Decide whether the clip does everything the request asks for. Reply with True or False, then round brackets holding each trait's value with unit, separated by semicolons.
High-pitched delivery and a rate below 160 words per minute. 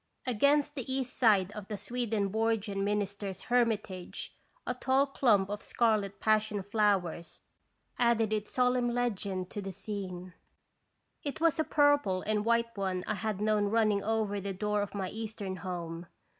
True (210 Hz; 150 wpm)